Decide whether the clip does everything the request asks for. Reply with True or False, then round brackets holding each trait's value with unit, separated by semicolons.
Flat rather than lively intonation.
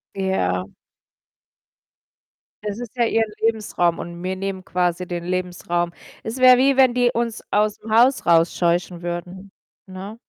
False (4.5 semitones)